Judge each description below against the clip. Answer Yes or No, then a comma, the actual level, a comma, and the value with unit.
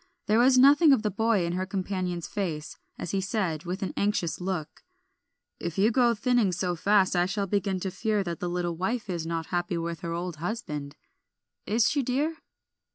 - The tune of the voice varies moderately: Yes, average, 3.9 semitones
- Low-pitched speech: No, high, 190 Hz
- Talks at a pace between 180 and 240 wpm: Yes, average, 200 wpm